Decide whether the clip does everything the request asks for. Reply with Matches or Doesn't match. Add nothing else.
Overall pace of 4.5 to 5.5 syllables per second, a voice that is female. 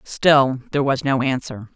Matches